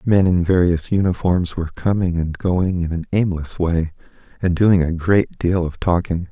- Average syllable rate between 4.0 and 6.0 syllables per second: Yes, 4.6 syllables/s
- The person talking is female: No, male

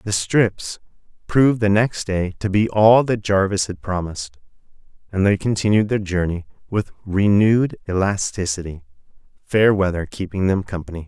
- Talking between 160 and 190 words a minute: No, average, 140 wpm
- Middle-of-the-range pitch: No, low, 100 Hz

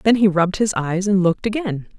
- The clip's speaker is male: No, female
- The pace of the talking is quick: Yes, fast, 240 wpm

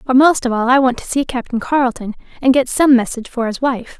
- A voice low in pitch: No, very high, 250 Hz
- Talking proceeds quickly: Yes, fast, 255 wpm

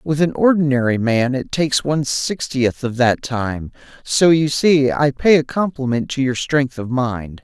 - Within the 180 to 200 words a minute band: Yes, average, 185 wpm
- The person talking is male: Yes, male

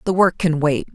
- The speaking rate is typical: No, fast, 255 wpm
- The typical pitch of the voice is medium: Yes, medium, 165 Hz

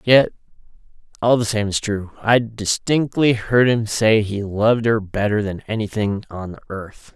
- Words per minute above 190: No, average, 160 wpm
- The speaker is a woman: No, male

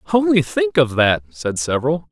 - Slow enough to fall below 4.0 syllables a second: No, 5.2 syllables/s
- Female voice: No, male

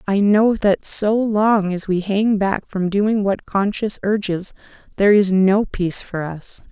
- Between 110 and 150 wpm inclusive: No, average, 180 wpm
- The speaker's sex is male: No, female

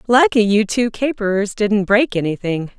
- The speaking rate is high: No, average, 150 wpm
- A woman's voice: Yes, female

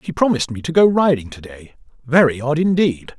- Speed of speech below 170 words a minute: No, fast, 205 wpm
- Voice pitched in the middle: Yes, medium, 145 Hz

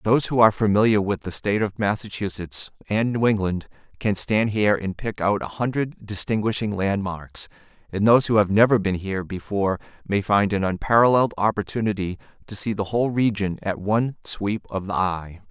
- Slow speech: No, average, 170 wpm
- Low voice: Yes, low, 105 Hz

